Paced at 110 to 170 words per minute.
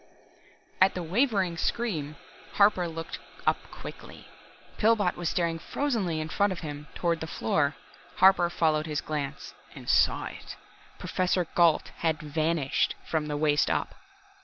Yes: average, 140 wpm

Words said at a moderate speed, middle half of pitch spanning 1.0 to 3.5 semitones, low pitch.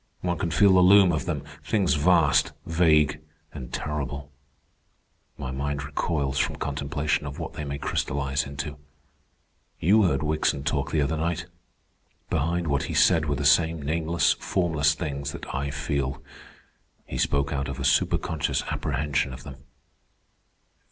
Yes: average, 145 wpm; average, 2.7 semitones; very low, 75 Hz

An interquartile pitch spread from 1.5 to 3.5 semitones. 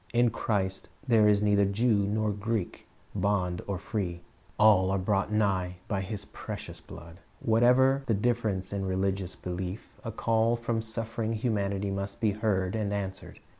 Yes: average, 2.7 semitones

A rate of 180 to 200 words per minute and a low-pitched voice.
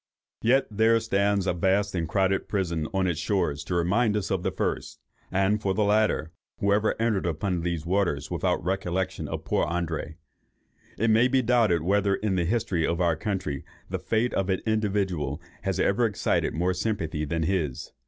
Yes: average, 185 wpm; very low, 95 Hz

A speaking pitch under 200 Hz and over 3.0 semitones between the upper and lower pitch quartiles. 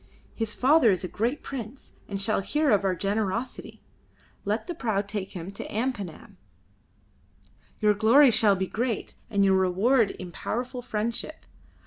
No: high, 215 Hz; average, 4.0 semitones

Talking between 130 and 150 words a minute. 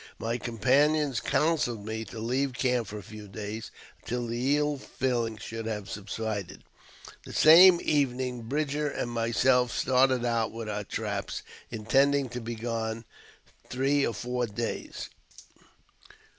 Yes: average, 145 wpm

